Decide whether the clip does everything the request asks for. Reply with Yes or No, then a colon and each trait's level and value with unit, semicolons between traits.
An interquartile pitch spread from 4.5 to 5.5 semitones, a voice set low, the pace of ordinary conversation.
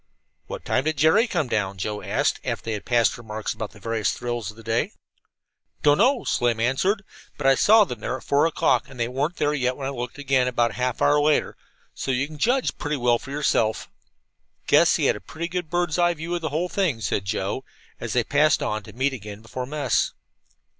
No: average, 5.1 semitones; low, 130 Hz; fast, 220 wpm